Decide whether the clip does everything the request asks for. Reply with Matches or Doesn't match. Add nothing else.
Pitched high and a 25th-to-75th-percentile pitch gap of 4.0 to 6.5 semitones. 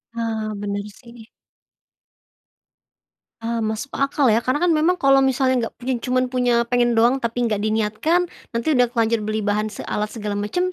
Doesn't match